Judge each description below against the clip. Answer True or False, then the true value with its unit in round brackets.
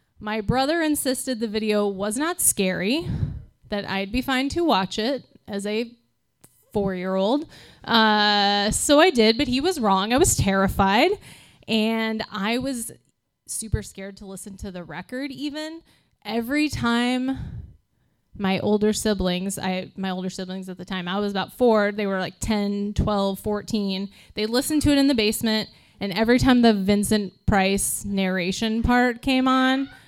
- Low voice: False (215 Hz)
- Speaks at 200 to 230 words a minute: False (160 wpm)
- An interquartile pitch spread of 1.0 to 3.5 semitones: False (4.5 semitones)